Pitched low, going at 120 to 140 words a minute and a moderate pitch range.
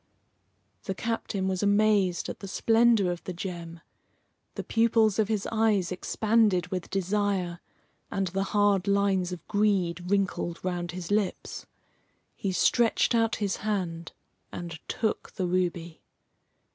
No: high, 195 Hz; slow, 135 wpm; average, 3.0 semitones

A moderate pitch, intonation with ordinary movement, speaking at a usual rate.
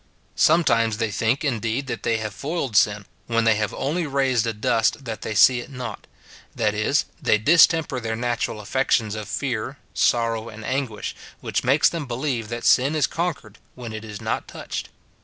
No: low, 120 Hz; average, 3.7 semitones; average, 185 wpm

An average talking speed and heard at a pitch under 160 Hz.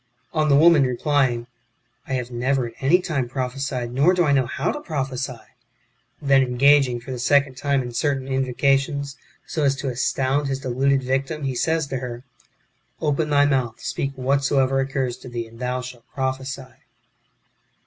Yes: average, 180 wpm; low, 135 Hz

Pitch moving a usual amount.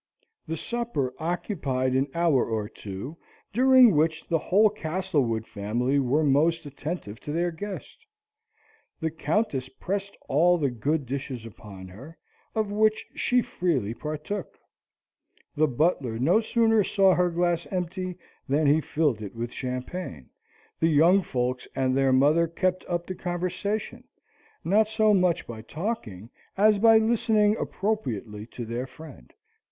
No: wide, 6.8 semitones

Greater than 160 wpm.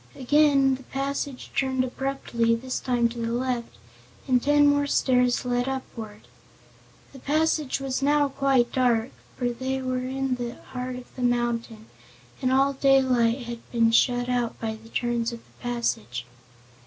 No: average, 155 wpm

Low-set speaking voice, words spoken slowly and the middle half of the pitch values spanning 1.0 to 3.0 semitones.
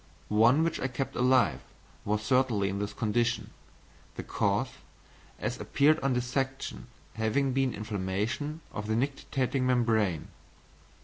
No: low, 120 Hz; slow, 125 wpm; average, 4.2 semitones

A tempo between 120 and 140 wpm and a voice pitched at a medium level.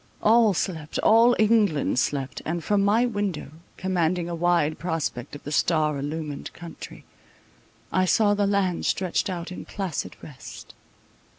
Yes: slow, 135 wpm; medium, 175 Hz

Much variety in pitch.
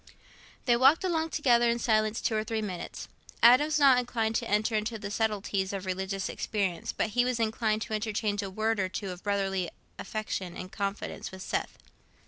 No: average, 3.1 semitones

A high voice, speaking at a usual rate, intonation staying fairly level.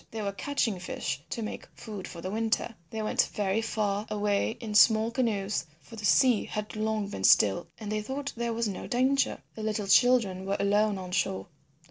Yes: high, 215 Hz; average, 195 wpm; narrow, 2.3 semitones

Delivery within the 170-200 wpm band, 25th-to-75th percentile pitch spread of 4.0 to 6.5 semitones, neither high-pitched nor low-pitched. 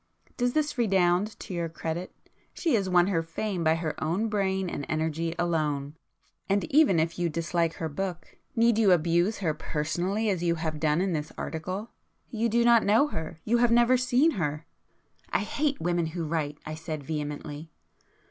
Yes: average, 180 wpm; average, 4.9 semitones; medium, 175 Hz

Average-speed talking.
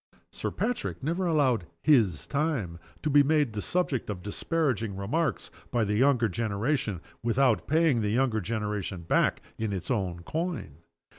Yes: average, 150 wpm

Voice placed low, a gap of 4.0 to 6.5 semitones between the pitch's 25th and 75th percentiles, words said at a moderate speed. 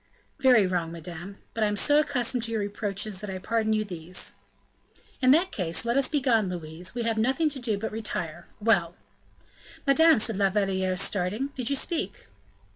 No: high, 215 Hz; average, 5.0 semitones; average, 185 wpm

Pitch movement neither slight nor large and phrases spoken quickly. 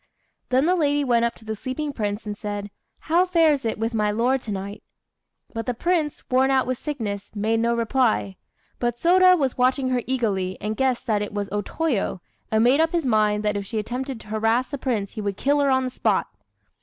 Yes: average, 4.3 semitones; fast, 220 wpm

